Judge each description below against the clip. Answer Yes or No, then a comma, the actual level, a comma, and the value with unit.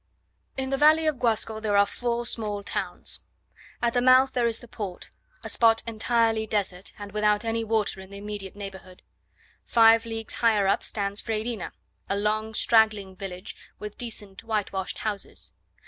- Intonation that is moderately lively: No, narrow, 2.3 semitones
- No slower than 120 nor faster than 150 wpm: No, average, 165 wpm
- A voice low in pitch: No, high, 220 Hz